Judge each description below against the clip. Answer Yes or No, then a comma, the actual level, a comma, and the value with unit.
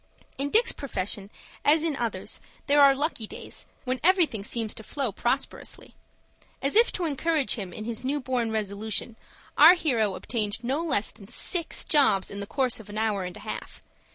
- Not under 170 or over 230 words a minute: Yes, average, 180 wpm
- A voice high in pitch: Yes, high, 245 Hz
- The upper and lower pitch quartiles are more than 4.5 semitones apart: Yes, average, 5.3 semitones